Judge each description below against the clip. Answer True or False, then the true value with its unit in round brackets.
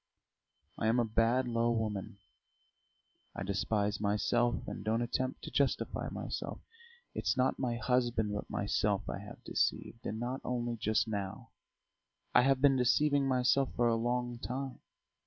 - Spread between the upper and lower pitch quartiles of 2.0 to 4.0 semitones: True (2.7 semitones)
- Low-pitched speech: True (120 Hz)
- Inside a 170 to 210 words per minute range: False (150 wpm)